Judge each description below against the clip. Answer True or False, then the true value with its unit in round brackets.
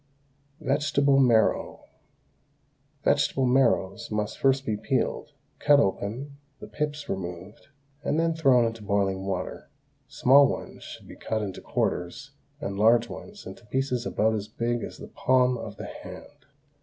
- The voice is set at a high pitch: False (120 Hz)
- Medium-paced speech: True (145 wpm)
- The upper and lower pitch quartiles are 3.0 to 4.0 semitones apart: False (4.8 semitones)